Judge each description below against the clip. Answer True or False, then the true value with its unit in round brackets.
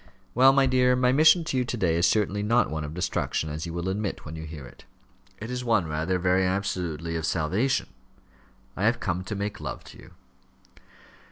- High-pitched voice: False (95 Hz)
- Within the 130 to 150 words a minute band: False (205 wpm)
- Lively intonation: True (6.8 semitones)